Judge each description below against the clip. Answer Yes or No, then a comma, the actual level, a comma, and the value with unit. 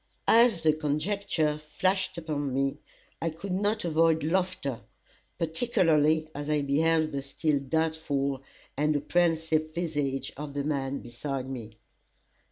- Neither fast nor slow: No, slow, 125 wpm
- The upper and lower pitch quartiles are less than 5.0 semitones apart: Yes, average, 2.7 semitones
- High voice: No, medium, 155 Hz